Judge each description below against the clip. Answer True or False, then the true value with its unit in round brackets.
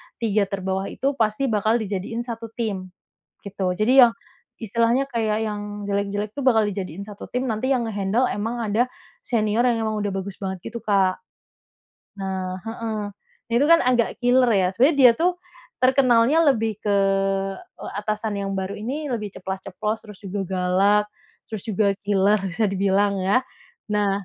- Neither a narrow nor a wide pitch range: True (3.0 semitones)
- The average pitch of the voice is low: False (215 Hz)